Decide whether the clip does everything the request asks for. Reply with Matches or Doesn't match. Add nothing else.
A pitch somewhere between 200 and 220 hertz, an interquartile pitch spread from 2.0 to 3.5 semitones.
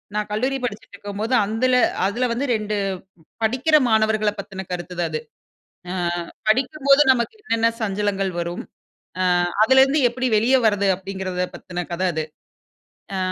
Doesn't match